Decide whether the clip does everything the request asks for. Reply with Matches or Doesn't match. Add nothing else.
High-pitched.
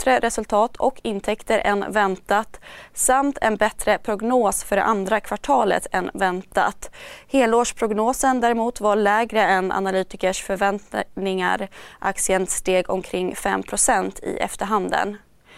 Matches